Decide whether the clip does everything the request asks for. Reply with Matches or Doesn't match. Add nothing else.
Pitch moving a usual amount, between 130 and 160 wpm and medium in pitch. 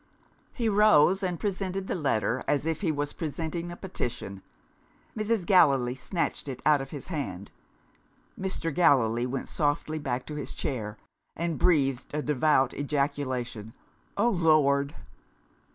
Matches